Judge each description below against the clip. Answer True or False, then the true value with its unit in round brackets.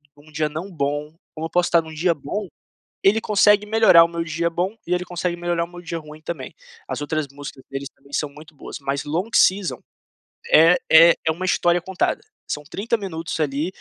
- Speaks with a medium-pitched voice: True (165 Hz)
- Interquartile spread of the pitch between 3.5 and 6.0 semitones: False (2.9 semitones)